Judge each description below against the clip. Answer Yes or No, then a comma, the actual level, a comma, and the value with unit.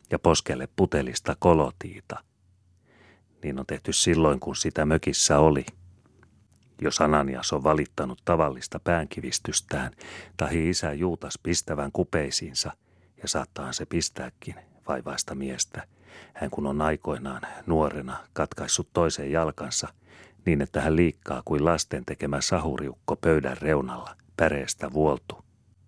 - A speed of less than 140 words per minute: Yes, average, 115 wpm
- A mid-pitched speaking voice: No, very low, 80 Hz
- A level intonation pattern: No, average, 3.6 semitones